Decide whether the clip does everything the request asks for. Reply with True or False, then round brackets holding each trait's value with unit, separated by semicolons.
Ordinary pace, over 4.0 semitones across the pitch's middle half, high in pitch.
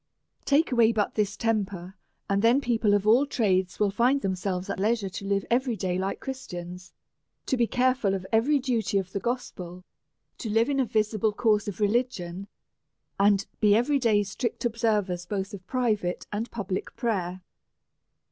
False (170 wpm; 3.7 semitones; 210 Hz)